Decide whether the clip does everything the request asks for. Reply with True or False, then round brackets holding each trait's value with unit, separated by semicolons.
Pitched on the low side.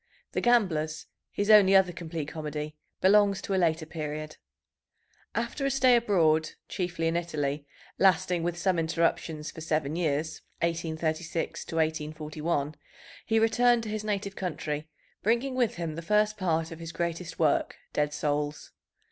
False (165 Hz)